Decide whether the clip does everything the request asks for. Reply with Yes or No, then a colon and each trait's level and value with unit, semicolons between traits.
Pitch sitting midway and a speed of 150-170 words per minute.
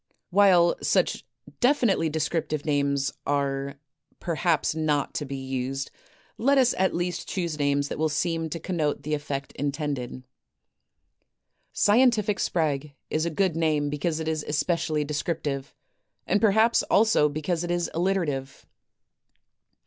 No: medium, 155 Hz; slow, 135 wpm